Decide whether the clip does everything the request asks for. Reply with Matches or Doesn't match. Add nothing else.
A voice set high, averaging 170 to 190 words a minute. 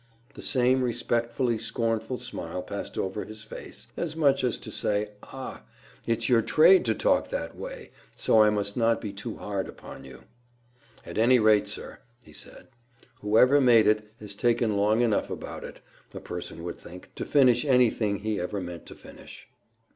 Doesn't match